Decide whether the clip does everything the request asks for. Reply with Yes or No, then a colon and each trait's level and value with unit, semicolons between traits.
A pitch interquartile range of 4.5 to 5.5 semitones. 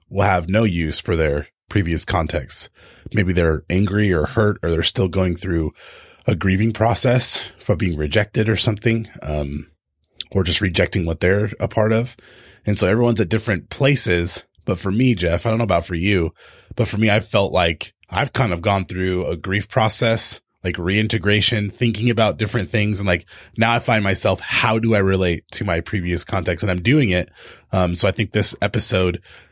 No: average, 3.8 semitones